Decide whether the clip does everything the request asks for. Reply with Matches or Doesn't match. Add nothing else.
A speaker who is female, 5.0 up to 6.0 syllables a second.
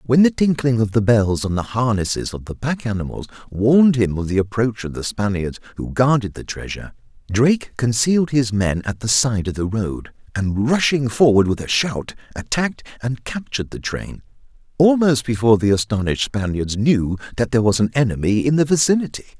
Doesn't match